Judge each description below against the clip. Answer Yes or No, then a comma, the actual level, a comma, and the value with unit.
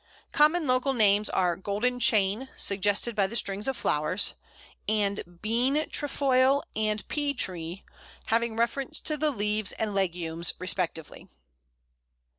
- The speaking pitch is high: Yes, high, 215 Hz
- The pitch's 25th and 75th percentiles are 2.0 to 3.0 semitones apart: No, average, 4.8 semitones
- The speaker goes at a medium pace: No, slow, 125 wpm